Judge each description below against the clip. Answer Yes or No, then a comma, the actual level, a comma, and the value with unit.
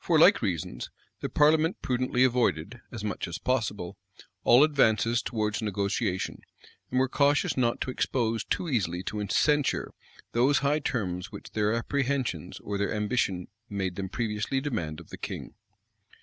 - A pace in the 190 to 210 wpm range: No, average, 150 wpm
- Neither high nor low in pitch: No, low, 115 Hz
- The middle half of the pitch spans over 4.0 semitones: Yes, average, 4.6 semitones